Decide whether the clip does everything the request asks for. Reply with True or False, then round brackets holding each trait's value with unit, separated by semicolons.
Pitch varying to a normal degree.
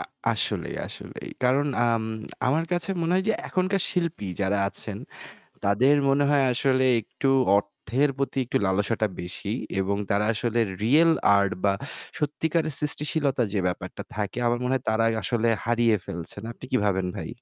False (6.2 semitones)